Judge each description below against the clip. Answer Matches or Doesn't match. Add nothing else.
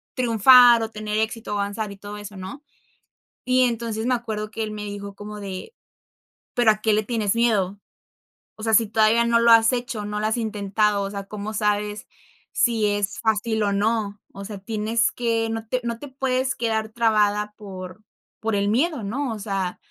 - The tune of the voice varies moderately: Doesn't match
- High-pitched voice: Matches